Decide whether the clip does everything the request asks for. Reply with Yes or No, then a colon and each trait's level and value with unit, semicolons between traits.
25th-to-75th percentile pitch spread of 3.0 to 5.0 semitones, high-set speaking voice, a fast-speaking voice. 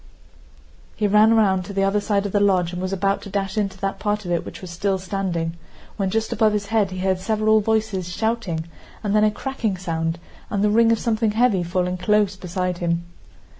No: narrow, 2.6 semitones; high, 195 Hz; fast, 215 wpm